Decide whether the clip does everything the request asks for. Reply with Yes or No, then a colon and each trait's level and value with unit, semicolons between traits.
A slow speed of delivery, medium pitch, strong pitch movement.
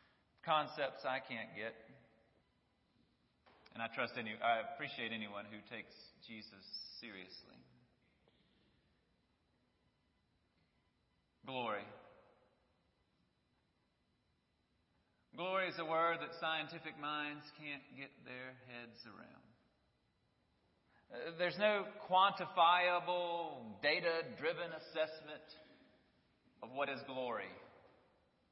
Yes: slow, 80 wpm; medium, 150 Hz; wide, 6.9 semitones